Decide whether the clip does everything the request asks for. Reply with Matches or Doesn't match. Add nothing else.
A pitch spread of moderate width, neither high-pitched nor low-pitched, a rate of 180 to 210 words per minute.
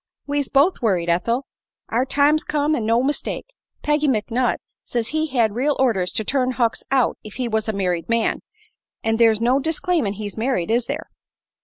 Doesn't match